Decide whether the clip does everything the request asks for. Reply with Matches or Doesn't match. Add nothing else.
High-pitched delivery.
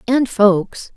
Matches